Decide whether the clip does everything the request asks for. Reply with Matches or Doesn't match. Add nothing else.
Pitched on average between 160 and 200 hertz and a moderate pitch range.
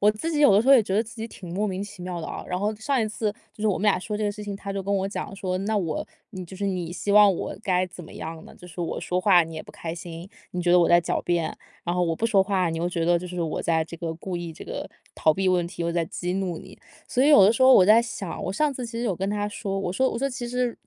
Matches